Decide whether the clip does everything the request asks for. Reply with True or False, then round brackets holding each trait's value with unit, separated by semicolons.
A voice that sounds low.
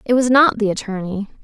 False (220 Hz)